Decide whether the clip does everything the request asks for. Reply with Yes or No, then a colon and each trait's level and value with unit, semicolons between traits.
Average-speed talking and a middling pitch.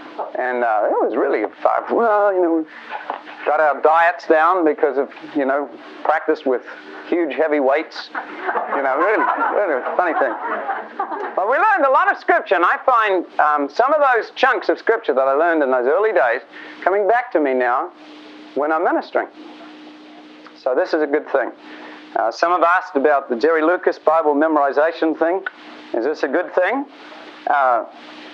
Yes: average, 180 wpm; medium, 160 Hz